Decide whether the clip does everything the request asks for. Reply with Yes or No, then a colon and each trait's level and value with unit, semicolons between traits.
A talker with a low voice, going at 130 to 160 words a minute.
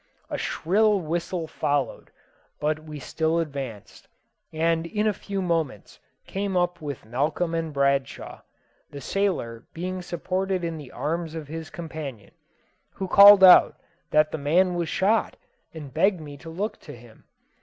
No: medium, 165 Hz; average, 150 wpm